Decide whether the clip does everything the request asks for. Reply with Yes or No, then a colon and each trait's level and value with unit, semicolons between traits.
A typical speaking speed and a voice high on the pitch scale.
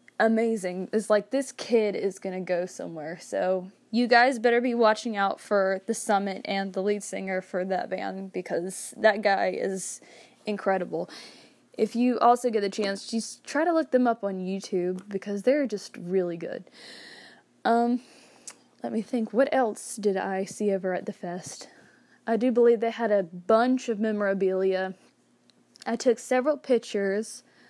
Yes: average, 165 wpm; high, 210 Hz